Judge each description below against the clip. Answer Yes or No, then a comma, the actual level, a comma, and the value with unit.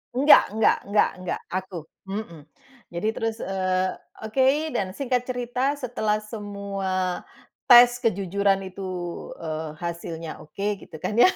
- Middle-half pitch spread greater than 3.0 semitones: Yes, average, 3.7 semitones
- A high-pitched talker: Yes, high, 200 Hz